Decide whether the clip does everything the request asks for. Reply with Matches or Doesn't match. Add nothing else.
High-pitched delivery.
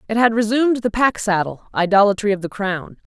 Matches